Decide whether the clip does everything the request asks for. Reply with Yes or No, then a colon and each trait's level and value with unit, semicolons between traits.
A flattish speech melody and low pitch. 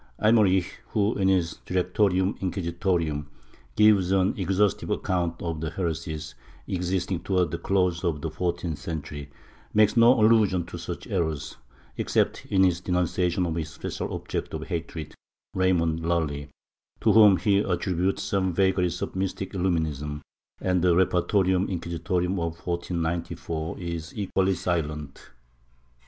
Yes: narrow, 2.3 semitones; very low, 90 Hz